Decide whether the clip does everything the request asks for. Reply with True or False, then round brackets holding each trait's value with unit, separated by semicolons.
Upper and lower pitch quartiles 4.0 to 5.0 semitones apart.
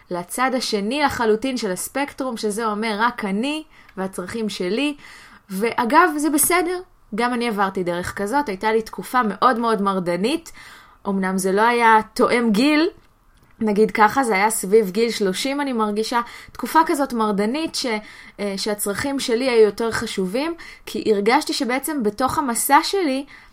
True (4.5 semitones)